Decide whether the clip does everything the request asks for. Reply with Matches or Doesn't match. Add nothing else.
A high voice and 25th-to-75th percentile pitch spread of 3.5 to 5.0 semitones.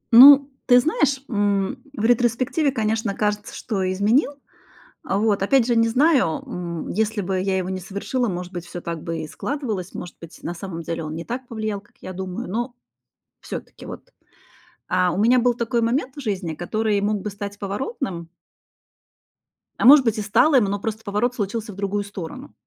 Matches